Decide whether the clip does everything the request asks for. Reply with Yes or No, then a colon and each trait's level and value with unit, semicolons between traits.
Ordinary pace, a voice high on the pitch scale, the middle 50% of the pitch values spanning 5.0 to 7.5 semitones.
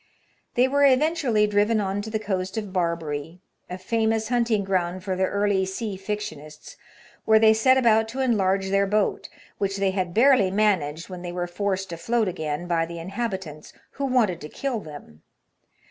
No: average, 180 wpm; high, 195 Hz; average, 3.7 semitones